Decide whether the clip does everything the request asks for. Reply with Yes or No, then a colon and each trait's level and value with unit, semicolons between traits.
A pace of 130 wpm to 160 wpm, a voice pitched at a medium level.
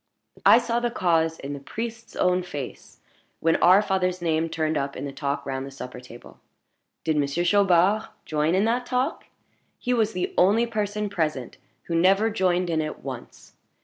No: average, 180 wpm; medium, 180 Hz